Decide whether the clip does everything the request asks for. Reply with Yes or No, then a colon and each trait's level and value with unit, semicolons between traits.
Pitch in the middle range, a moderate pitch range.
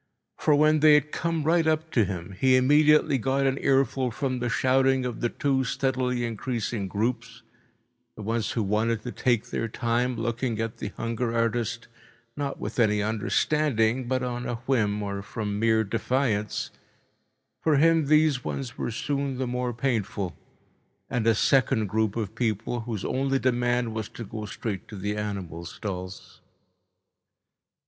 No: low, 120 Hz; average, 3.4 semitones